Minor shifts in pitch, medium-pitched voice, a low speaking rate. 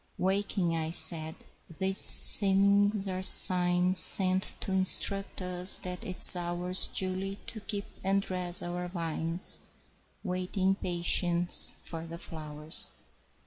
Yes: narrow, 1.8 semitones; medium, 180 Hz; slow, 120 wpm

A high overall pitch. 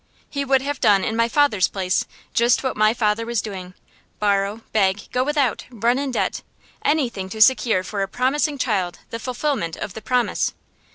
Yes: high, 230 Hz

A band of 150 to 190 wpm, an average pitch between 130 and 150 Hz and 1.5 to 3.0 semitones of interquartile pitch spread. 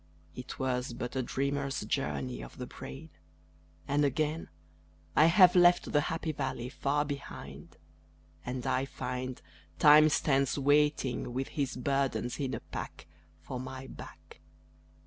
No: slow, 135 wpm; low, 135 Hz; narrow, 2.5 semitones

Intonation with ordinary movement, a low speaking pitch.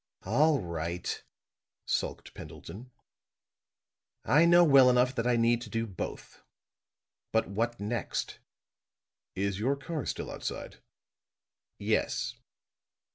Yes: average, 4.6 semitones; low, 120 Hz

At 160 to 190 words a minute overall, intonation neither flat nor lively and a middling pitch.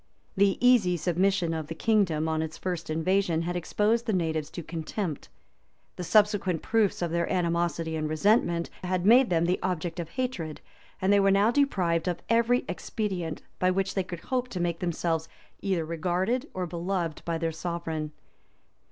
Yes: average, 170 wpm; average, 3.3 semitones; medium, 175 Hz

